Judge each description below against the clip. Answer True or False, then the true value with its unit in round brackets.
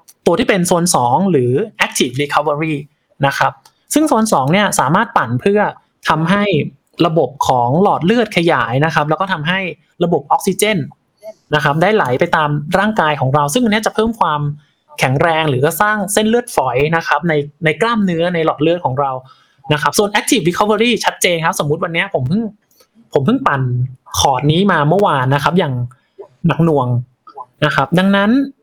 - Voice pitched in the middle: True (165 Hz)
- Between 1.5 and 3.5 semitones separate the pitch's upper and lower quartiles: False (5.6 semitones)